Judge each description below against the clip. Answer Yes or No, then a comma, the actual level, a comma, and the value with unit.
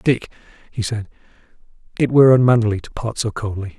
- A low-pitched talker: Yes, low, 110 Hz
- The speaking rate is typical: Yes, average, 160 wpm